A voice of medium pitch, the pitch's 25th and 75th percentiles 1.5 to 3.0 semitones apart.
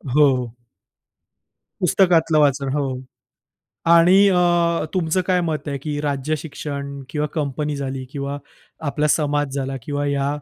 Yes: medium, 150 Hz; narrow, 2.5 semitones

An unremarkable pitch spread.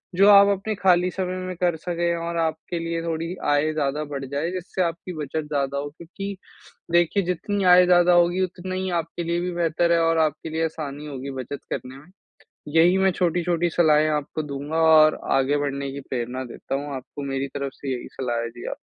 Yes: average, 3.7 semitones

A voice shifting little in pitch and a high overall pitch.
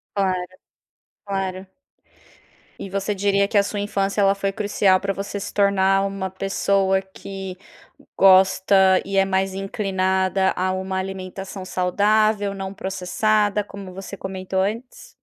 Yes: narrow, 0.9 semitones; high, 195 Hz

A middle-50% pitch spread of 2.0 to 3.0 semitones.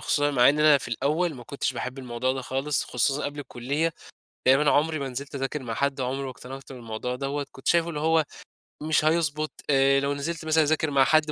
Yes: narrow, 2.5 semitones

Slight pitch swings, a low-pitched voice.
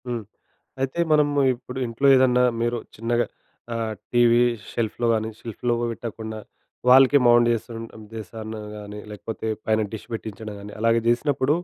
Yes: narrow, 2.0 semitones; low, 115 Hz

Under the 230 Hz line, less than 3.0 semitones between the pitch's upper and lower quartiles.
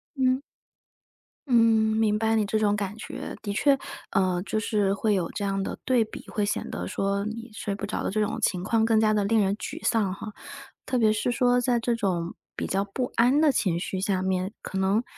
Yes: high, 215 Hz; narrow, 2.5 semitones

